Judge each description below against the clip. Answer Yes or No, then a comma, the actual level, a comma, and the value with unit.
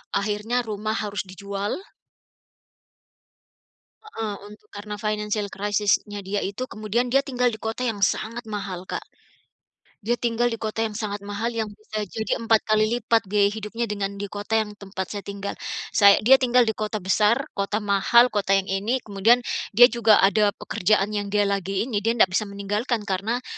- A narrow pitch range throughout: Yes, narrow, 2.0 semitones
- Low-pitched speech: No, high, 210 Hz